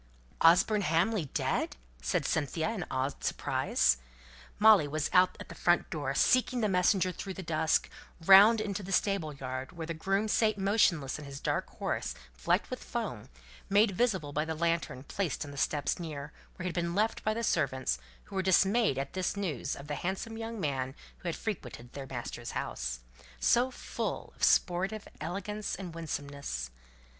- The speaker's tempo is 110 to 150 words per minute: No, average, 175 wpm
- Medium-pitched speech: Yes, medium, 170 Hz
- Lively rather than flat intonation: Yes, wide, 5.9 semitones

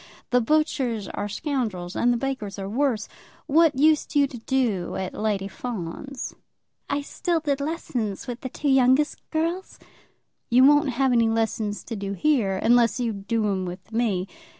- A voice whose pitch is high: Yes, high, 240 Hz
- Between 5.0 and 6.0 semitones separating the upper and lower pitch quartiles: Yes, average, 5.3 semitones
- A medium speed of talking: Yes, average, 165 wpm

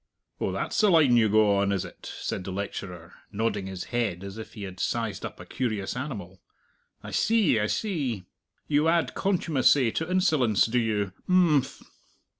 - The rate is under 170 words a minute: No, average, 175 wpm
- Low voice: Yes, low, 115 Hz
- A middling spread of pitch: No, wide, 7.2 semitones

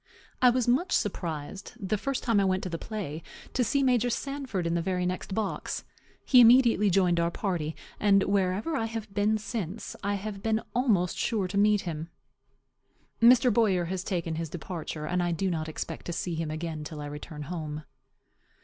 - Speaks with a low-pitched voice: No, high, 195 Hz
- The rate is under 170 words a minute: No, average, 190 wpm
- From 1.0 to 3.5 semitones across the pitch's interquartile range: No, average, 4.8 semitones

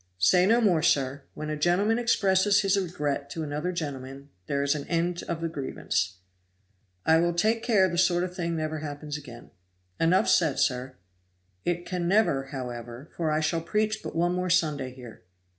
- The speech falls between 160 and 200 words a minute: Yes, average, 180 wpm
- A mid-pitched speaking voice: Yes, medium, 165 Hz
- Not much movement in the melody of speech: No, average, 4.3 semitones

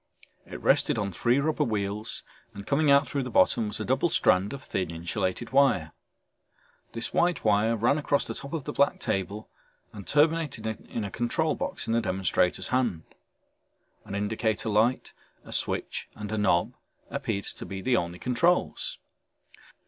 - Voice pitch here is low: Yes, low, 110 Hz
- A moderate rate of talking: Yes, average, 165 wpm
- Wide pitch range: Yes, wide, 5.7 semitones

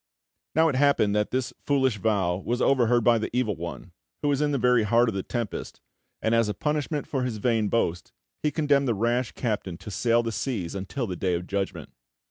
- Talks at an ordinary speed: No, fast, 220 wpm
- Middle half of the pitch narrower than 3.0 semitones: No, average, 4.4 semitones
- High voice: No, low, 115 Hz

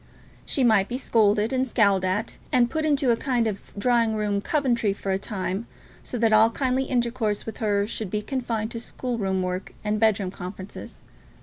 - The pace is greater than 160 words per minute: Yes, average, 195 wpm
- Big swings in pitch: No, average, 3.2 semitones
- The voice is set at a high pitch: Yes, high, 220 Hz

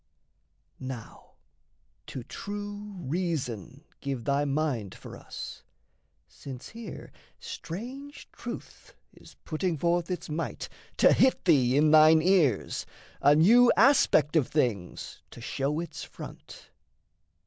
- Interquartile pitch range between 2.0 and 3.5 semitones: No, wide, 5.6 semitones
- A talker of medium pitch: Yes, medium, 155 Hz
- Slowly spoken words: Yes, slow, 115 wpm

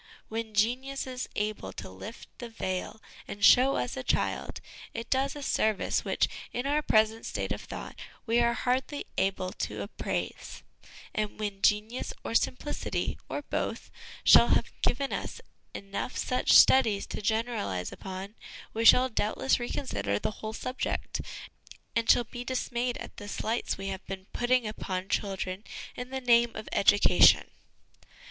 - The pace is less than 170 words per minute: Yes, average, 155 wpm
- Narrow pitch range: No, average, 3.7 semitones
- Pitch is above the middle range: Yes, high, 225 Hz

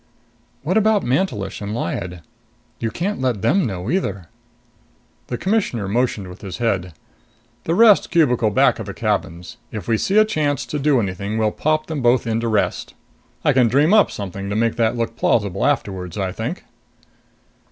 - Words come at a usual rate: Yes, average, 175 wpm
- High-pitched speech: No, low, 115 Hz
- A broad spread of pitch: Yes, wide, 7.2 semitones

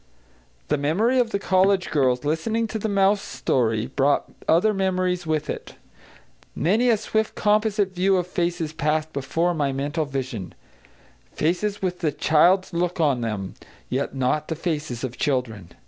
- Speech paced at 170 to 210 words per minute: No, average, 155 wpm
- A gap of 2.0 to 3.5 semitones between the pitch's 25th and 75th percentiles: No, wide, 5.6 semitones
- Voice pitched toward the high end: No, medium, 165 Hz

